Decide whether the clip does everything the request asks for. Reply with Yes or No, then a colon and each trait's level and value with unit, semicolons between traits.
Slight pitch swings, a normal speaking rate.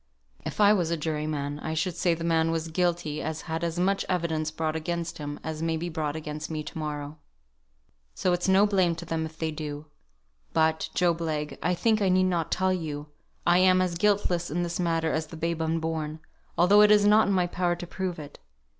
No: narrow, 2.3 semitones; fast, 220 wpm